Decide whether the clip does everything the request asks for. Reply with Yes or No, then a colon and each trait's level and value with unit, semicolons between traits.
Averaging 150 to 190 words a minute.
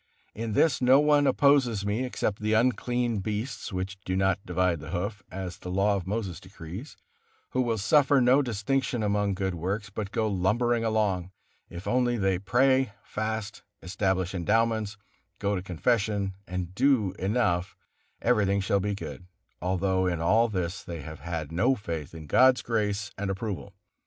Yes: average, 160 wpm